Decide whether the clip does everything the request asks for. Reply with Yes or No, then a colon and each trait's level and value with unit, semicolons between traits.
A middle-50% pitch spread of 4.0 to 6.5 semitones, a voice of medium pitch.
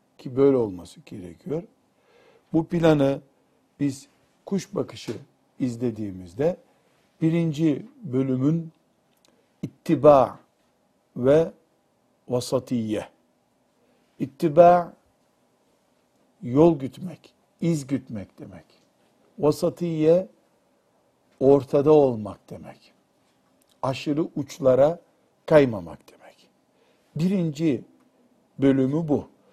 Yes: average, 4.4 semitones; medium, 145 Hz